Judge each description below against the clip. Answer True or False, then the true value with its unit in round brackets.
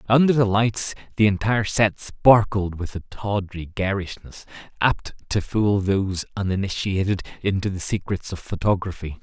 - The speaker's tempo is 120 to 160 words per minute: True (135 wpm)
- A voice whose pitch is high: False (100 Hz)